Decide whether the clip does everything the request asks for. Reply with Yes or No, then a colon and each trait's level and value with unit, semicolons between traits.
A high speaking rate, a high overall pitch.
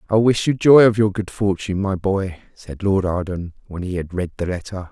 No: fast, 230 wpm; very low, 95 Hz